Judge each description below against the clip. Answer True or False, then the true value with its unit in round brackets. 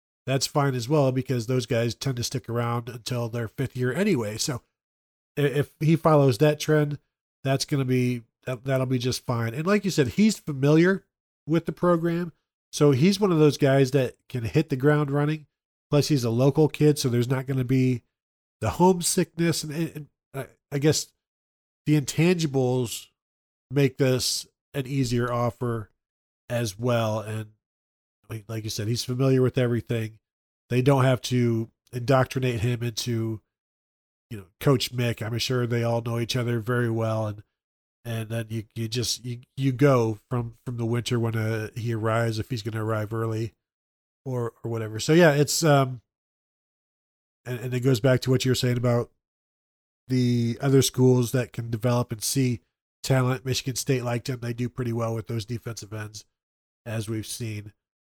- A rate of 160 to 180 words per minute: True (175 wpm)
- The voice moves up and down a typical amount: True (3.3 semitones)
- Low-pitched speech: True (125 Hz)